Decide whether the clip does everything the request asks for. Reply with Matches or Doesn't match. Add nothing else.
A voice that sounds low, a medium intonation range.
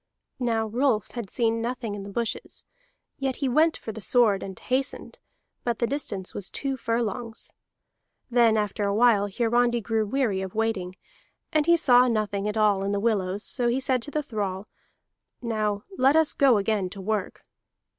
Doesn't match